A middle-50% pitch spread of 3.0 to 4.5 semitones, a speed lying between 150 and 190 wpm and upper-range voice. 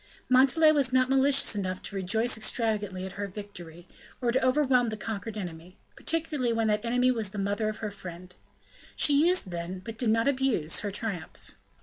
No: average, 5.0 semitones; average, 185 wpm; high, 220 Hz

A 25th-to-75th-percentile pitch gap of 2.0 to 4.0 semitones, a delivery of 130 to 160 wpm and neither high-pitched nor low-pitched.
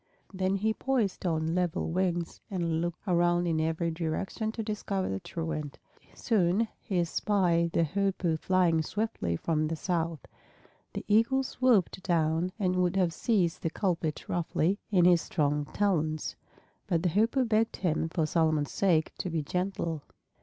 Yes: average, 3.2 semitones; average, 155 wpm; medium, 175 Hz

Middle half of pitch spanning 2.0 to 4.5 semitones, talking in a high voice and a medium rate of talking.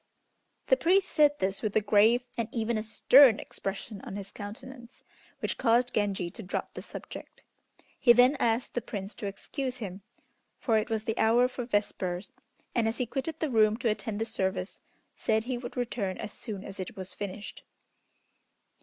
Yes: average, 3.3 semitones; high, 220 Hz; average, 180 wpm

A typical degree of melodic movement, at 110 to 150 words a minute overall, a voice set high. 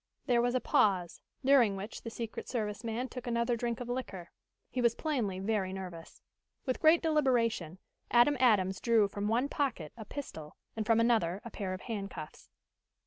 No: average, 4.0 semitones; average, 175 wpm; high, 230 Hz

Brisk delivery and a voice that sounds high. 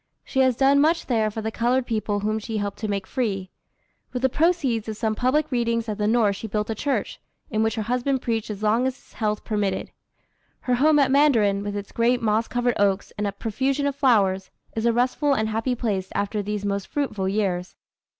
Yes: fast, 215 wpm; high, 225 Hz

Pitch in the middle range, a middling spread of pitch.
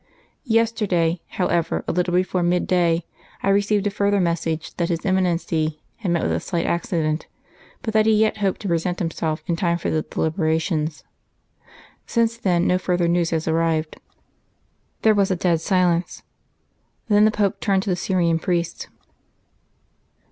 Yes: medium, 175 Hz; average, 3.0 semitones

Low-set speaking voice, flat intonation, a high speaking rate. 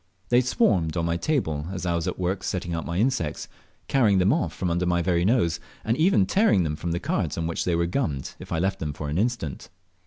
No: very low, 90 Hz; average, 4.1 semitones; fast, 245 wpm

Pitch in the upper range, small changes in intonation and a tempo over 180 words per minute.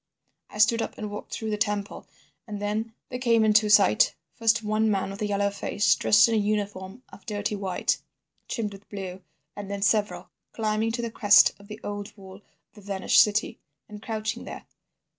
Yes: high, 210 Hz; narrow, 1.4 semitones; average, 190 wpm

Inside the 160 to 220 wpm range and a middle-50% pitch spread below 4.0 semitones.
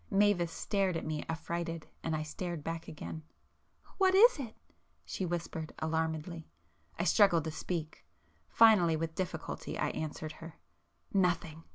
No: slow, 135 wpm; average, 2.7 semitones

